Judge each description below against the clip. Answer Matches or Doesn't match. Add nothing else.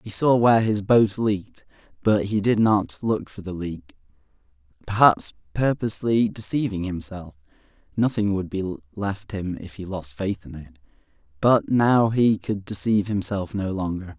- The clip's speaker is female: Doesn't match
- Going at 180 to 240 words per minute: Doesn't match